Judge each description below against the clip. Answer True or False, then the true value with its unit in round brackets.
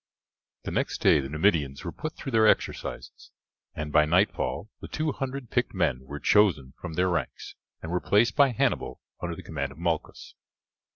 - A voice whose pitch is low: True (90 Hz)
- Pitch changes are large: True (6.6 semitones)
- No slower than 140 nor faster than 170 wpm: False (180 wpm)